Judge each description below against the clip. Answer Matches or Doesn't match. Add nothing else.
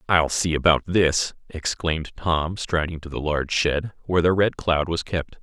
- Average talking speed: Matches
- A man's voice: Matches